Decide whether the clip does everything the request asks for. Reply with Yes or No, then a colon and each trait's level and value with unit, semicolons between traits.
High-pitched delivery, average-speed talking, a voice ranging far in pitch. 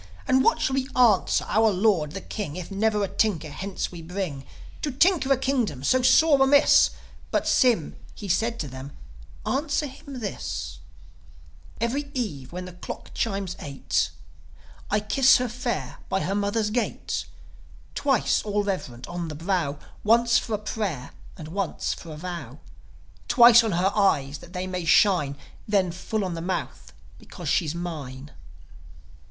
Yes: high, 195 Hz; average, 160 wpm; wide, 6.1 semitones